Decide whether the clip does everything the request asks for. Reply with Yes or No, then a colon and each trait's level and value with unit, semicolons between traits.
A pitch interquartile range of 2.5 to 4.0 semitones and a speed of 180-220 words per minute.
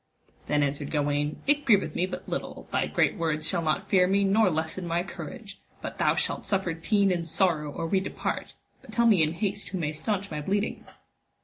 No: average, 4.4 semitones; fast, 205 wpm